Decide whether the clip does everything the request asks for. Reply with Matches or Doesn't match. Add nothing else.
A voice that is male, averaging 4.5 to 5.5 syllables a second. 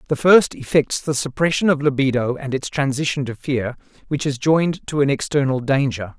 Matches